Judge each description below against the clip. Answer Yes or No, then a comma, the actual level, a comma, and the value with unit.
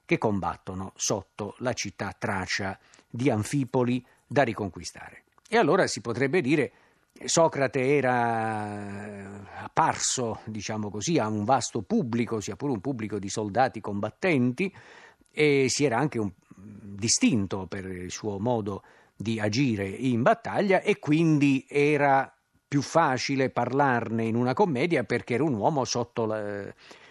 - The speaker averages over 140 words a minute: No, average, 135 wpm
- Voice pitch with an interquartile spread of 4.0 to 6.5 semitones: Yes, average, 5.2 semitones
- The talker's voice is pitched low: Yes, low, 120 Hz